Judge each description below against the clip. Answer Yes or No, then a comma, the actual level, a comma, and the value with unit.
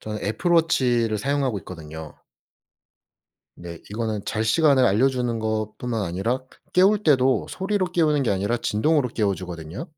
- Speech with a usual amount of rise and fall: No, wide, 5.7 semitones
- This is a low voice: Yes, low, 115 Hz